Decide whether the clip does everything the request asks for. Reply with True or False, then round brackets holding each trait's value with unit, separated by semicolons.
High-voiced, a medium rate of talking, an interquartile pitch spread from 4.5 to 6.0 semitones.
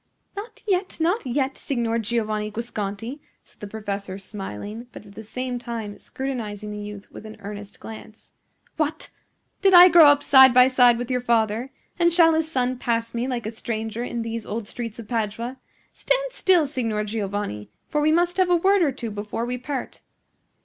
True (235 Hz; 185 wpm; 4.8 semitones)